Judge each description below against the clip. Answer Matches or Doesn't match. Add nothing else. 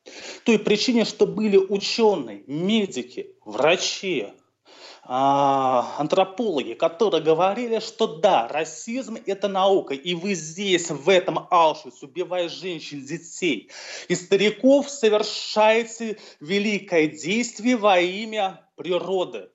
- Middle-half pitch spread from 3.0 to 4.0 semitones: Doesn't match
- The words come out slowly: Matches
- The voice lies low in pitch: Doesn't match